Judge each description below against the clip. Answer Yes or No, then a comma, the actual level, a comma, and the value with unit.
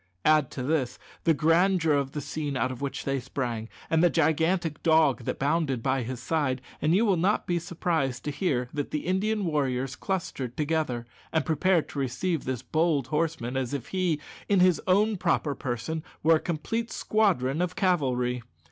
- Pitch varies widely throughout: No, average, 4.6 semitones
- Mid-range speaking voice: Yes, medium, 155 Hz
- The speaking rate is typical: Yes, average, 185 wpm